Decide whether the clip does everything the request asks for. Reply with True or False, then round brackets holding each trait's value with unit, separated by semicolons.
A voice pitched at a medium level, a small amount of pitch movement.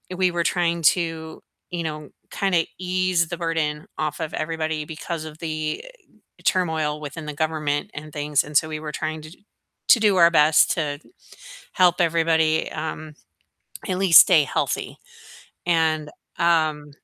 True (160 Hz; 1.9 semitones)